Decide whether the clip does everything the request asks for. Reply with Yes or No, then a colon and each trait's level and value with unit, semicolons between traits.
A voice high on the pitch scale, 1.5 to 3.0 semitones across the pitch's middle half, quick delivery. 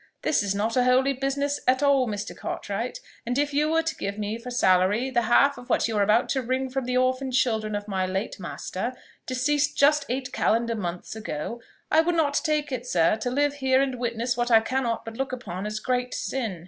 No: very high, 250 Hz; average, 3.8 semitones; fast, 225 wpm